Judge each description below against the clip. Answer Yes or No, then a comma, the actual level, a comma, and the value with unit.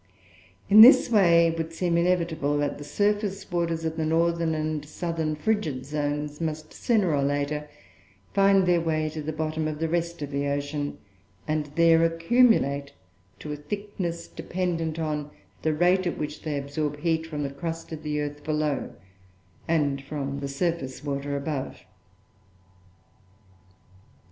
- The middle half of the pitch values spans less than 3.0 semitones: Yes, narrow, 2.5 semitones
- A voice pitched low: No, medium, 155 Hz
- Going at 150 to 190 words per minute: Yes, average, 155 wpm